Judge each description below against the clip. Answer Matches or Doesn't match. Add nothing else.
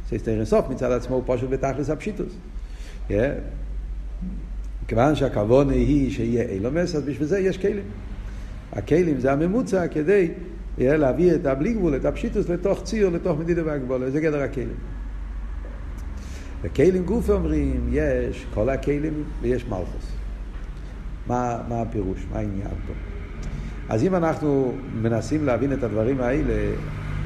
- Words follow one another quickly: Doesn't match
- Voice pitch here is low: Matches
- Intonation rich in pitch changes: Matches